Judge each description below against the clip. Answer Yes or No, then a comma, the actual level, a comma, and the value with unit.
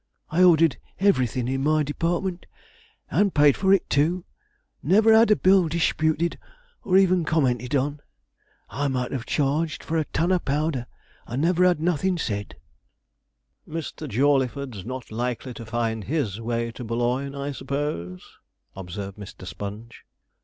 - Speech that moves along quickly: No, average, 145 wpm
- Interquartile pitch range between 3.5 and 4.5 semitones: No, wide, 5.6 semitones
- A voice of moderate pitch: Yes, medium, 145 Hz